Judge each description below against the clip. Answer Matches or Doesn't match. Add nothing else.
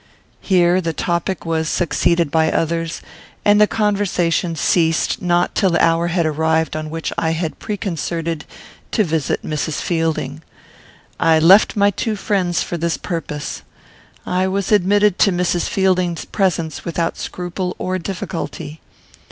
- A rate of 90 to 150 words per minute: Matches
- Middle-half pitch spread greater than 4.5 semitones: Doesn't match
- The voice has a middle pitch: Matches